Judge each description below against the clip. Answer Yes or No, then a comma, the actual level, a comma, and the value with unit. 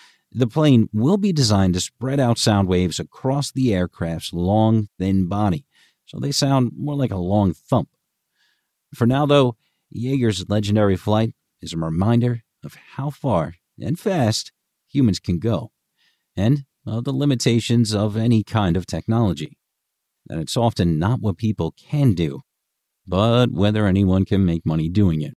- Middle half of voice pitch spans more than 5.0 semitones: Yes, wide, 5.4 semitones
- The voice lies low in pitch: Yes, low, 110 Hz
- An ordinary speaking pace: Yes, average, 160 wpm